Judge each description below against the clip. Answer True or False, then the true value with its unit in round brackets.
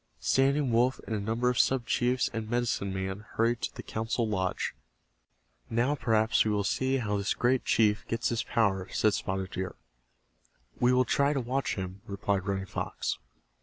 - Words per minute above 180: False (175 wpm)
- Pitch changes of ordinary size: True (3.8 semitones)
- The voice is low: True (115 Hz)